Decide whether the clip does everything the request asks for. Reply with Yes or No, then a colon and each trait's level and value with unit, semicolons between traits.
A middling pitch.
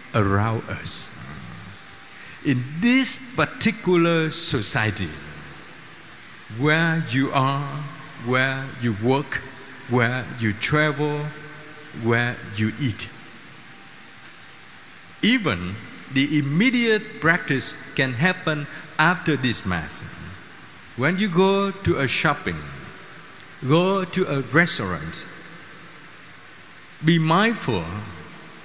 Yes: medium, 145 Hz